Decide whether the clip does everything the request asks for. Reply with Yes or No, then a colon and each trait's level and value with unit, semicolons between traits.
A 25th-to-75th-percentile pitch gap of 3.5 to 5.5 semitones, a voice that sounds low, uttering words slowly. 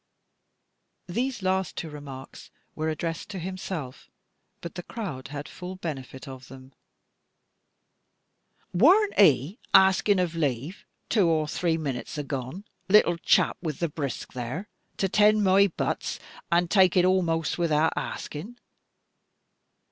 No: average, 4.5 semitones; medium, 170 Hz; slow, 125 wpm